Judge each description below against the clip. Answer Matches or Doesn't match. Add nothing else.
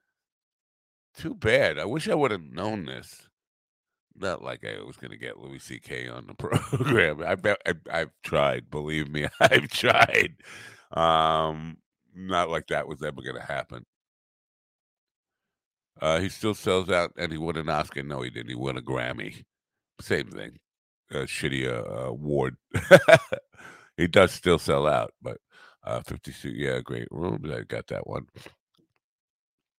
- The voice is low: Matches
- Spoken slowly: Doesn't match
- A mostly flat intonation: Doesn't match